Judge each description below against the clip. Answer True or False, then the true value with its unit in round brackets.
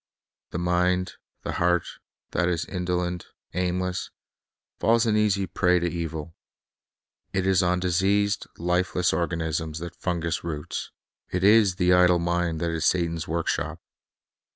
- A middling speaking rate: False (130 wpm)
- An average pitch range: False (1.4 semitones)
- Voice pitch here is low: True (90 Hz)